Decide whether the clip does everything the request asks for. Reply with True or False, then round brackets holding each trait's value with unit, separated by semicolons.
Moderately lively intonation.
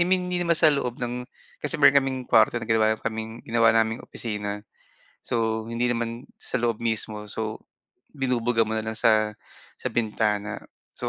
False (1.9 semitones)